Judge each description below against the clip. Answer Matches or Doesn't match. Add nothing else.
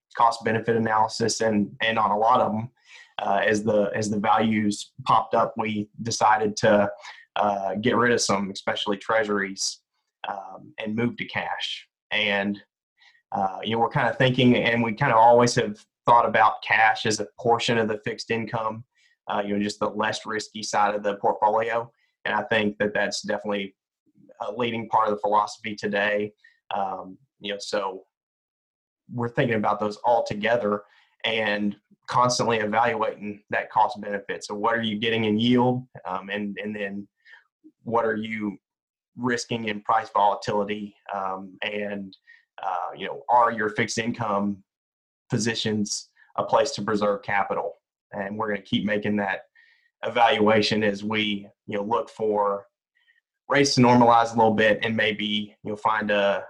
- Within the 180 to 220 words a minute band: Doesn't match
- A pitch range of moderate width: Doesn't match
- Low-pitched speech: Matches